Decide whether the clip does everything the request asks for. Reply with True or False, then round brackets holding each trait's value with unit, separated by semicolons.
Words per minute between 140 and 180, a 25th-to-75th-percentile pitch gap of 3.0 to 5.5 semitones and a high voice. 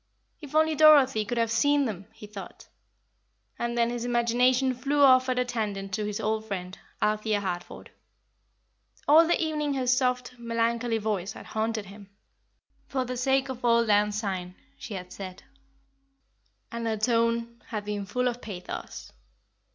True (160 wpm; 3.3 semitones; 235 Hz)